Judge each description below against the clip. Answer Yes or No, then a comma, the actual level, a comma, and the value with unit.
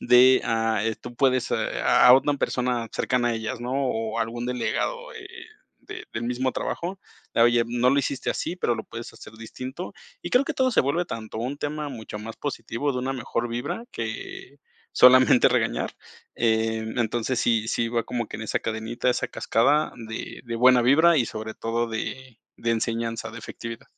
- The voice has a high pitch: No, low, 120 Hz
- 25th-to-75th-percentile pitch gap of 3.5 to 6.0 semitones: No, narrow, 2.5 semitones